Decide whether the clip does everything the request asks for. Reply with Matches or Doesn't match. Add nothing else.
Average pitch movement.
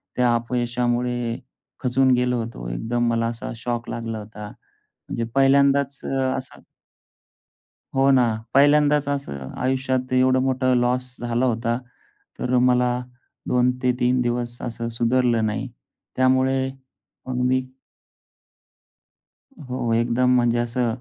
Doesn't match